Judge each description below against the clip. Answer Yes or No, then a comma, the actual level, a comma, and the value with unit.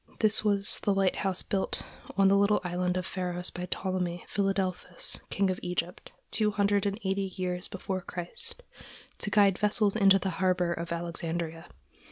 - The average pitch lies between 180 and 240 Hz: Yes, high, 190 Hz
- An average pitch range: No, narrow, 1.9 semitones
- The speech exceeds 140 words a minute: Yes, average, 160 wpm